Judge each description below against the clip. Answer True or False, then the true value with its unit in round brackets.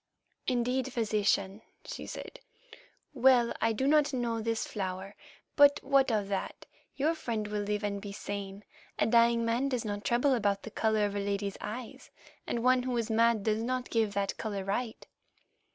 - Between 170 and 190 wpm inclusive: True (175 wpm)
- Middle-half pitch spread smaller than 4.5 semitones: True (3.4 semitones)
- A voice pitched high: True (225 Hz)